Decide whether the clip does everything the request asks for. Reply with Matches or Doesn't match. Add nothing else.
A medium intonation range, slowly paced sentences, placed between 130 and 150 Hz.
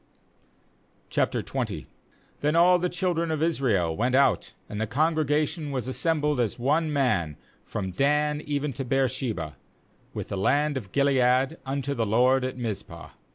Doesn't match